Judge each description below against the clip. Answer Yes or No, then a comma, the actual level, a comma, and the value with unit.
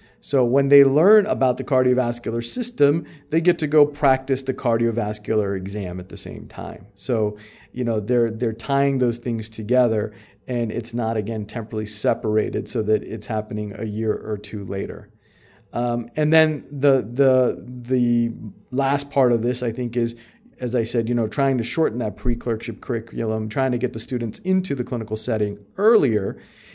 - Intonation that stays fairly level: No, average, 3.4 semitones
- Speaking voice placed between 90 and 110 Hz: No, low, 120 Hz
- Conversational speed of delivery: Yes, average, 175 wpm